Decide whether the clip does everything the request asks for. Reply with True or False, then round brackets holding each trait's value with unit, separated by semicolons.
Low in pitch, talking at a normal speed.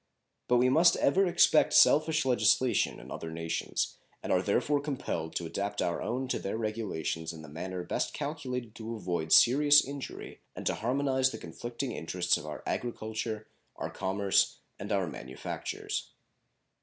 True (110 Hz; 155 wpm)